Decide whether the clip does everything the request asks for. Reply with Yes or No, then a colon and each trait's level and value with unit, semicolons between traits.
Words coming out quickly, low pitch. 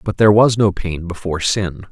Yes: fast, 220 wpm; very low, 95 Hz